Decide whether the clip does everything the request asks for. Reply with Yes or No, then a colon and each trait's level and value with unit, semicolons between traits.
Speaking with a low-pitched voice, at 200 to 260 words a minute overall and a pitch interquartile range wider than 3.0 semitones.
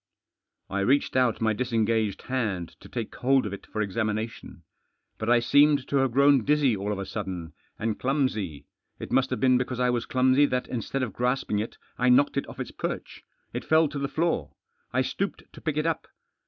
Yes: low, 125 Hz; fast, 205 wpm; average, 4.1 semitones